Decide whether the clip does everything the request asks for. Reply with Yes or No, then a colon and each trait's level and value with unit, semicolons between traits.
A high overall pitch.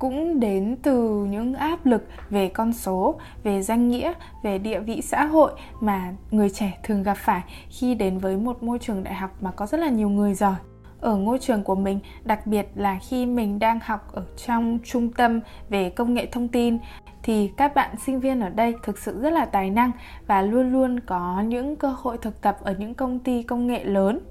Yes: high, 225 Hz